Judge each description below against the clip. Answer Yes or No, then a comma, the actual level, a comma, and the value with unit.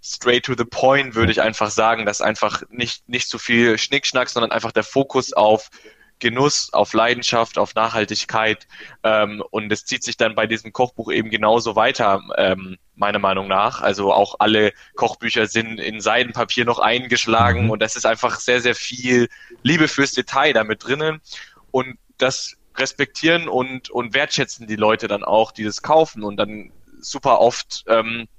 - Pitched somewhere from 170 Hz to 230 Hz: No, low, 115 Hz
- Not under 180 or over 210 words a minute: No, average, 170 wpm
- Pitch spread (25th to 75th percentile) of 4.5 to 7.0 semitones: No, average, 2.9 semitones